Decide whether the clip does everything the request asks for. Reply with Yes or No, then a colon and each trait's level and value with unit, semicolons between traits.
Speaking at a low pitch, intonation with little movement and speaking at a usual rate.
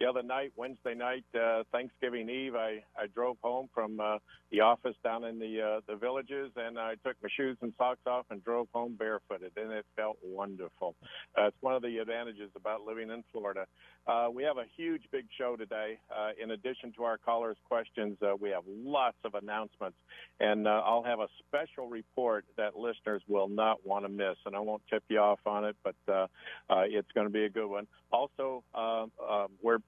No: low, 110 Hz; narrow, 2.2 semitones; fast, 210 wpm